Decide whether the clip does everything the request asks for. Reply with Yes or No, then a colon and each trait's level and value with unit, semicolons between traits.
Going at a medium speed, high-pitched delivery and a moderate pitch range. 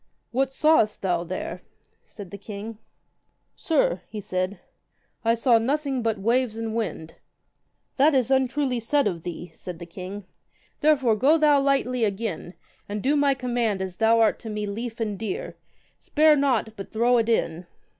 Yes: average, 165 wpm; high, 230 Hz; average, 4.7 semitones